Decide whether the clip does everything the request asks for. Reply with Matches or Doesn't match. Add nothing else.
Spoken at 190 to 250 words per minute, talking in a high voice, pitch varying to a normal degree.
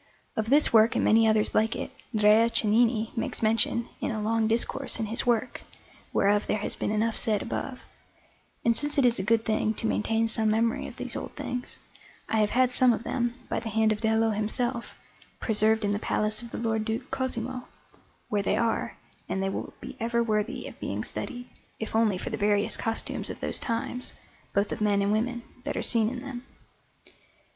Doesn't match